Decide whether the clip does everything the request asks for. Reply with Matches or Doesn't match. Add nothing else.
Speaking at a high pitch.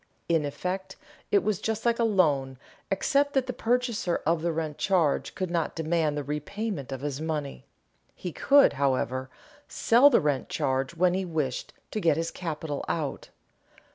Doesn't match